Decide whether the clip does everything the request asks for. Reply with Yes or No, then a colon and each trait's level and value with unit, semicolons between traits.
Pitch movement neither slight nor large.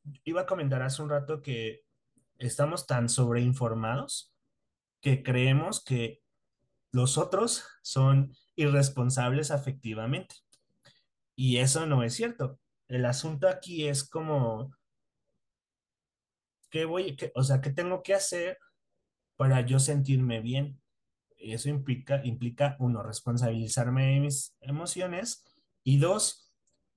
Yes: average, 3.2 semitones